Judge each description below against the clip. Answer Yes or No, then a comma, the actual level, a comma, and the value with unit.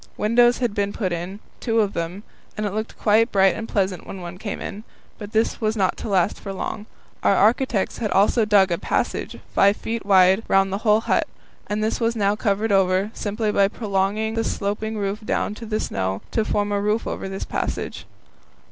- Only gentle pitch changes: Yes, narrow, 2.1 semitones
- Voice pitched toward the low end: No, high, 205 Hz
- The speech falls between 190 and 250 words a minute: Yes, fast, 205 wpm